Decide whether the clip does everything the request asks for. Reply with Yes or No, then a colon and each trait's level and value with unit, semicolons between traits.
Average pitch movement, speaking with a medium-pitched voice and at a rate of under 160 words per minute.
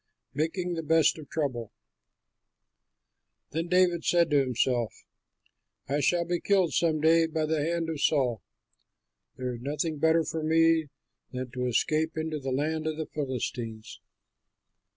Yes: average, 3.5 semitones; medium, 155 Hz; average, 145 wpm